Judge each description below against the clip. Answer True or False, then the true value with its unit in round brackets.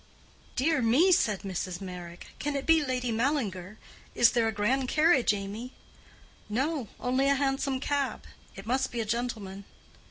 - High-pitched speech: True (245 Hz)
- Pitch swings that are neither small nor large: True (4.8 semitones)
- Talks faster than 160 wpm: False (150 wpm)